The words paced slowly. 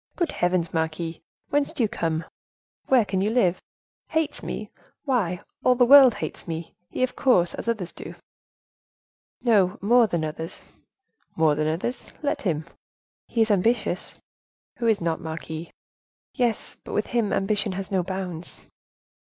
No: average, 150 wpm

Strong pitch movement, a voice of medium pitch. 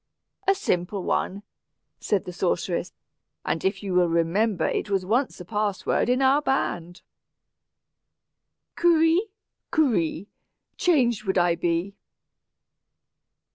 No: wide, 6.2 semitones; high, 195 Hz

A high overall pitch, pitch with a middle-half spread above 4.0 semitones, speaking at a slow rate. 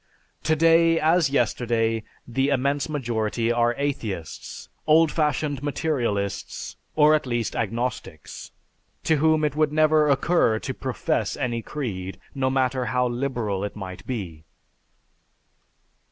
No: low, 130 Hz; average, 4.9 semitones; slow, 120 wpm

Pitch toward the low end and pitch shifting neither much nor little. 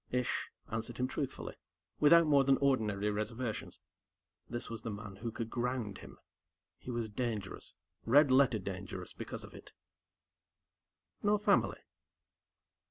Yes: low, 120 Hz; average, 3.8 semitones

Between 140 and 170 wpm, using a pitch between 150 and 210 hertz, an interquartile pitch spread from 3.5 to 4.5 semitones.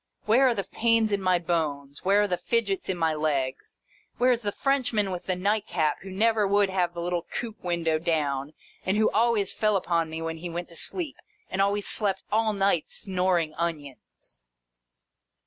No: average, 185 wpm; medium, 185 Hz; average, 4.2 semitones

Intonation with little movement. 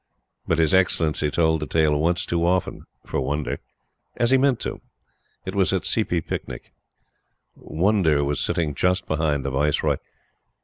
No: average, 3.7 semitones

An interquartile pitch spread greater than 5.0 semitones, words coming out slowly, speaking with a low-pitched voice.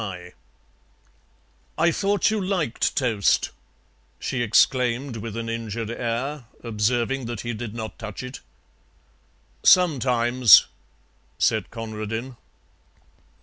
No: average, 2.7 semitones; slow, 95 wpm; low, 120 Hz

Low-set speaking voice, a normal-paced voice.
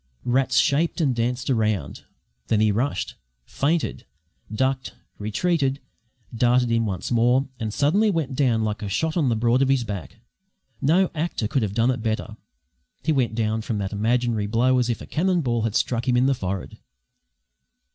Yes: low, 120 Hz; average, 175 wpm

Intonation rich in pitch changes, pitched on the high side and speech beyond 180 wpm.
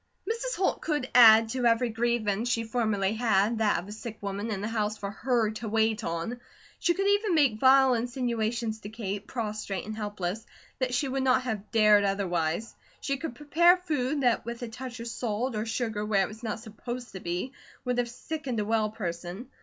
No: average, 3.1 semitones; high, 225 Hz; average, 200 wpm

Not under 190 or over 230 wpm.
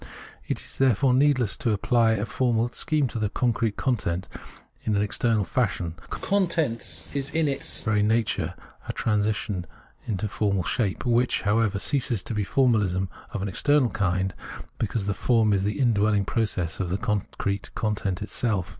No: average, 170 wpm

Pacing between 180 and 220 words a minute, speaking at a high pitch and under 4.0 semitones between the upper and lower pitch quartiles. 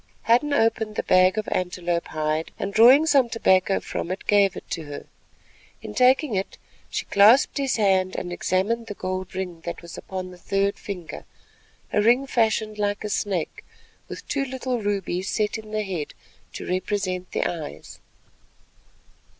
No: average, 165 wpm; high, 200 Hz; average, 3.6 semitones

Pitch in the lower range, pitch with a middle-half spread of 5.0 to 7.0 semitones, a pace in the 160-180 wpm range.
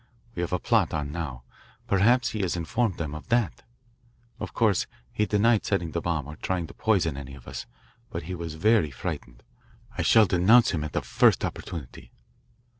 No: very low, 85 Hz; wide, 5.6 semitones; average, 190 wpm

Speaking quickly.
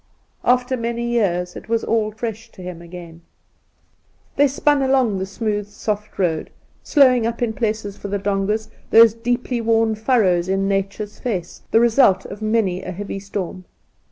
No: average, 165 wpm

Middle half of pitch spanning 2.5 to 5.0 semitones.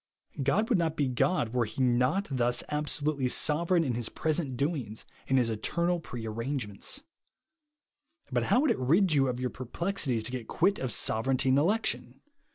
No: wide, 5.6 semitones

